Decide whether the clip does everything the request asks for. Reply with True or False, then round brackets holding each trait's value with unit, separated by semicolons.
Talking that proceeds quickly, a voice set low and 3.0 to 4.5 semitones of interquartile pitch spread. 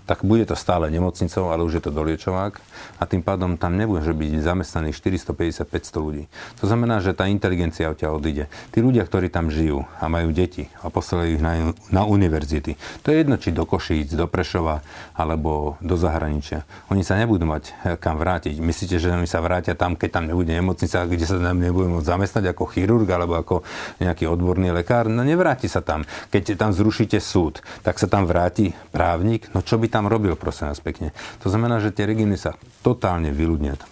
True (195 wpm; 90 Hz; 3.7 semitones)